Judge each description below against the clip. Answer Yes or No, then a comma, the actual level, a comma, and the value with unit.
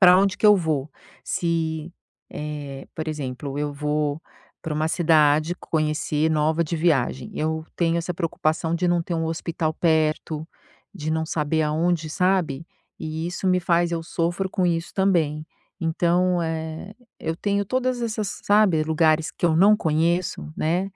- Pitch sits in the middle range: Yes, medium, 160 Hz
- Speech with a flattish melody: Yes, narrow, 2.2 semitones